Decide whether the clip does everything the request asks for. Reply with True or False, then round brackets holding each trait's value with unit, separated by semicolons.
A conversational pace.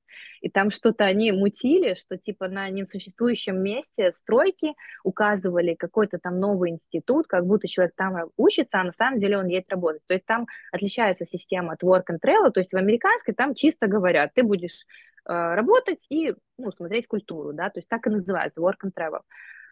False (185 wpm)